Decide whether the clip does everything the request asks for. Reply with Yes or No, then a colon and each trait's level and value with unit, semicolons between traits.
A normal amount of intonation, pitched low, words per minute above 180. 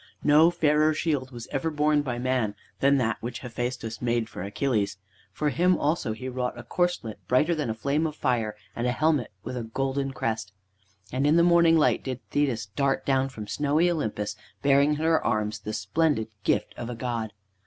Yes: average, 4.6 semitones; low, 130 Hz; average, 195 wpm